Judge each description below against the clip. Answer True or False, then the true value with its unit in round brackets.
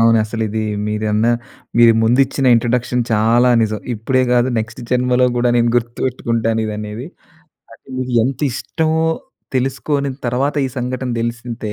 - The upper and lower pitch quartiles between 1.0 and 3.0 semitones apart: True (2.4 semitones)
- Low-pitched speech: True (120 Hz)